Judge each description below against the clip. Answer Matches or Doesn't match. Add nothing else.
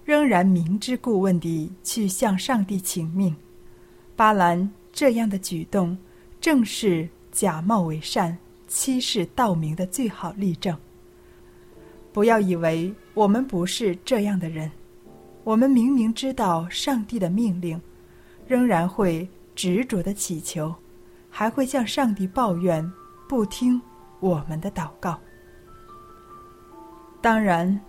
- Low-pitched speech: Doesn't match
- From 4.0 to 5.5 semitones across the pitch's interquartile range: Matches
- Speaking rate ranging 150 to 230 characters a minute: Matches